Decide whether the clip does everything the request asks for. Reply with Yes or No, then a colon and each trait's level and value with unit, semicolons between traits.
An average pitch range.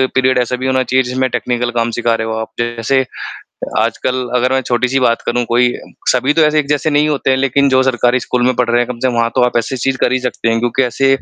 No: narrow, 1.6 semitones